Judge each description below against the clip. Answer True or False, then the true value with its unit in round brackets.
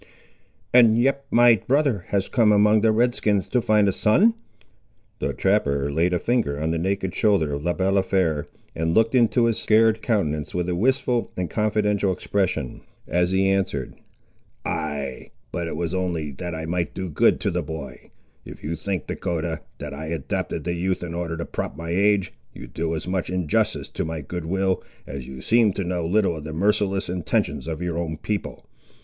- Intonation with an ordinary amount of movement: True (4.4 semitones)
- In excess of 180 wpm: True (190 wpm)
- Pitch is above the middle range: False (90 Hz)